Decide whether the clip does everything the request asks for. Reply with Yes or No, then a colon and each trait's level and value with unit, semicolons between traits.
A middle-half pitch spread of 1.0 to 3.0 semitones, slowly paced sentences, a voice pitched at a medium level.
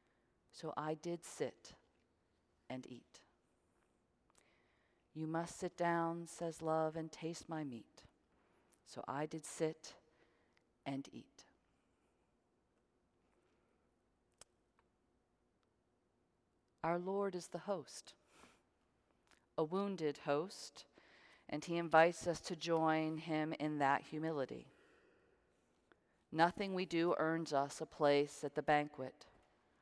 Yes: narrow, 2.6 semitones; slow, 100 wpm; medium, 160 Hz